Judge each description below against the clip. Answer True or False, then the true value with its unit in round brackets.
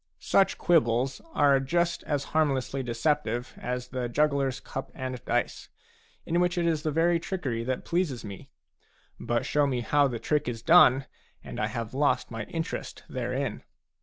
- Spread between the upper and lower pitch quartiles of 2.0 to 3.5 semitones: False (4.3 semitones)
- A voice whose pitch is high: False (135 Hz)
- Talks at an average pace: True (165 wpm)